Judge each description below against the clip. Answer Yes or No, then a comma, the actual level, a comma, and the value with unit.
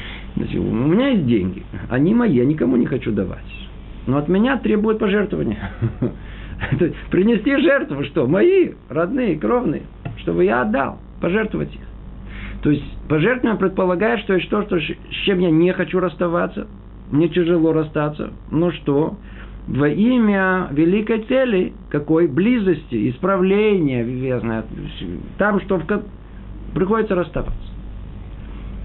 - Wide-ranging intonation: Yes, wide, 8.0 semitones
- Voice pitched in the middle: Yes, medium, 175 Hz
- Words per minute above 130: No, average, 125 wpm